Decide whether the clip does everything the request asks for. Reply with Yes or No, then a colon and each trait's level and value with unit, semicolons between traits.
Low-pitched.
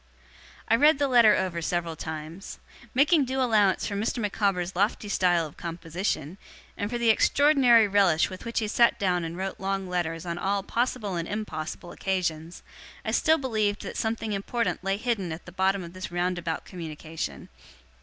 No: high, 195 Hz